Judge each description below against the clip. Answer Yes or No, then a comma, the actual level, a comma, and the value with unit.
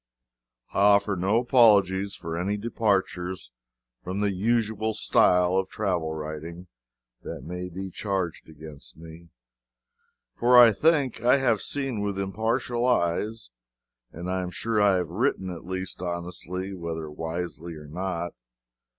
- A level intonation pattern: No, average, 3.8 semitones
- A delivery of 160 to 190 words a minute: No, slow, 135 wpm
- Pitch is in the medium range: No, very low, 95 Hz